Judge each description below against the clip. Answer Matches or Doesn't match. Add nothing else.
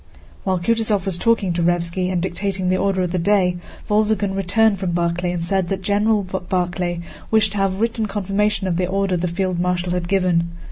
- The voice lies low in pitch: Doesn't match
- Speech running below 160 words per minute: Doesn't match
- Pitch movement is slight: Matches